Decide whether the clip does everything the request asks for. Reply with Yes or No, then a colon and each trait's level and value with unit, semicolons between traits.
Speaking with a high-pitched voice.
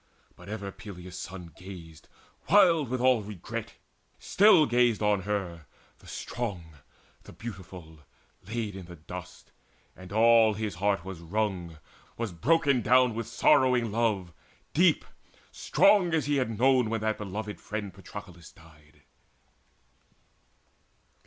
No: low, 105 Hz